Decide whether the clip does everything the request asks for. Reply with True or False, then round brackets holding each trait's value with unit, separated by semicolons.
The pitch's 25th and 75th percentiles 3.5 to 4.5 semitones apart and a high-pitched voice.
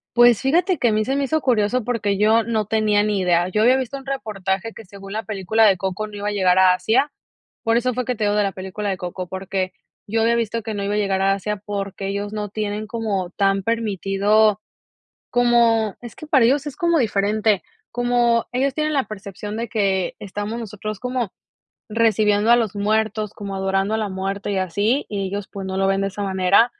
False (2.8 semitones; 210 Hz)